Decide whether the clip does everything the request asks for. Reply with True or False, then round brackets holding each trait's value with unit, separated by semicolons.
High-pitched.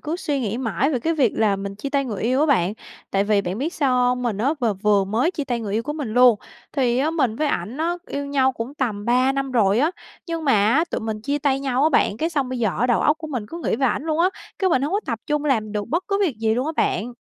True (255 Hz)